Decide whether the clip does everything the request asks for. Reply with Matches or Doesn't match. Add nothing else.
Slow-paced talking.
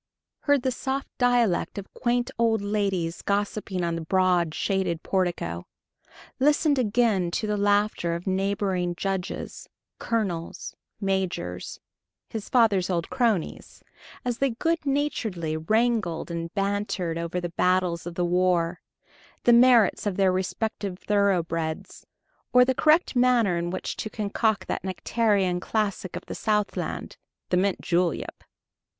Matches